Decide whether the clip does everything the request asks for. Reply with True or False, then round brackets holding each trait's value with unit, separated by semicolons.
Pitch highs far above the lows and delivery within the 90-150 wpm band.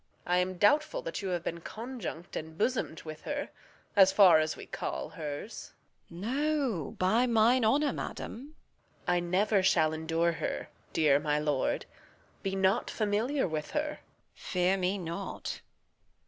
False (6.3 semitones; 160 wpm)